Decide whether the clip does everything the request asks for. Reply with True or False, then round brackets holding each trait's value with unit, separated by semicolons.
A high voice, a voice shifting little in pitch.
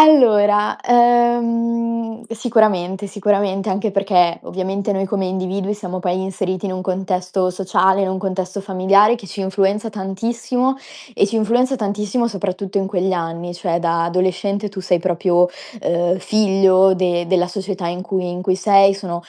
True (195 Hz; 2.2 semitones)